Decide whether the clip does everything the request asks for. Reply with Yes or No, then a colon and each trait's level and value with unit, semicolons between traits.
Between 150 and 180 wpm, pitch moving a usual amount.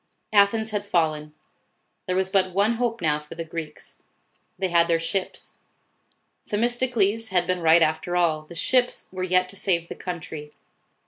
Yes: average, 170 wpm; average, 3.6 semitones